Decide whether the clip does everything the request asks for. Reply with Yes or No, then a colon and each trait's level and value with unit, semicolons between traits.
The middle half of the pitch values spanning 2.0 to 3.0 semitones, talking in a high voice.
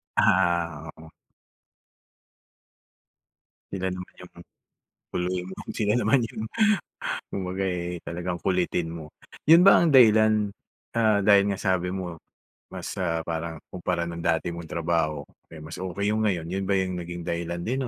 No: average, 2.7 semitones; very low, 90 Hz